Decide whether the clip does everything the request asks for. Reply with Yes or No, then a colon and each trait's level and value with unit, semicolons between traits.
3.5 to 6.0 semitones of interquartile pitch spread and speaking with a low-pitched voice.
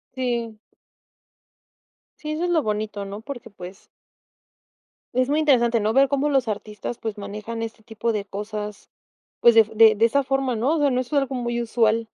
No: average, 3.8 semitones; high, 230 Hz